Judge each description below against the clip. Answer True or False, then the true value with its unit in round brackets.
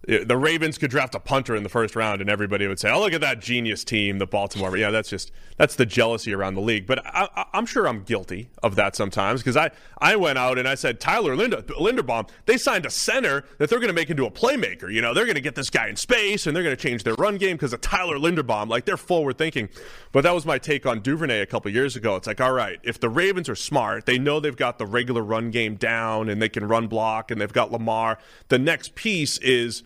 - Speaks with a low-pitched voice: True (120 Hz)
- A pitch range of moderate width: True (4.3 semitones)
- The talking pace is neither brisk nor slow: False (265 wpm)